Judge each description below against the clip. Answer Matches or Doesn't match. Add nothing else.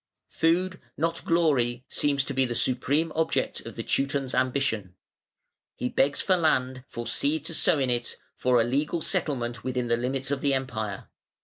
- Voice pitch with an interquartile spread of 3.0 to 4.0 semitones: Matches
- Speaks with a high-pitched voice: Doesn't match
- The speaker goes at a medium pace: Matches